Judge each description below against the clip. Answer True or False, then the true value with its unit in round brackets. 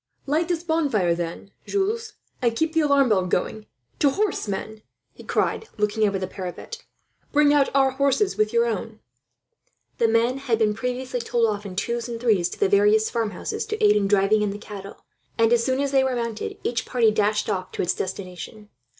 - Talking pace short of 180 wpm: False (200 wpm)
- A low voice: False (230 Hz)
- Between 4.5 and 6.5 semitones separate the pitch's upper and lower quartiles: True (5.1 semitones)